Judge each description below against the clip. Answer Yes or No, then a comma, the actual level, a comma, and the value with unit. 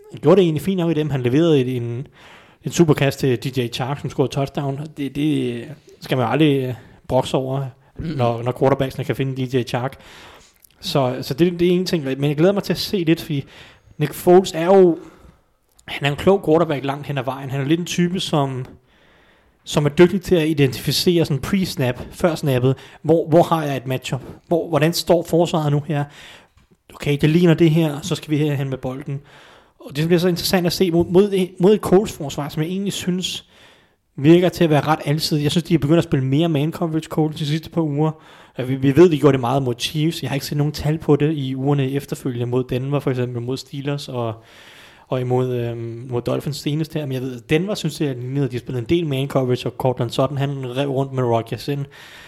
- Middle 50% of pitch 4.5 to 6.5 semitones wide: No, average, 3.8 semitones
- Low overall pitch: No, medium, 145 Hz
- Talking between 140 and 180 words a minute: No, fast, 225 wpm